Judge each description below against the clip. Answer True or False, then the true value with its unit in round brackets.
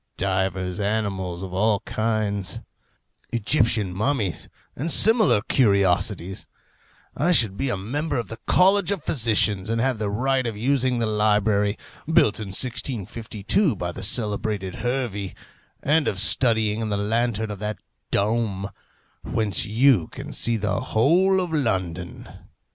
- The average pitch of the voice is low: True (110 Hz)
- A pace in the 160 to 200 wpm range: False (135 wpm)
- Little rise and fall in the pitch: False (4.1 semitones)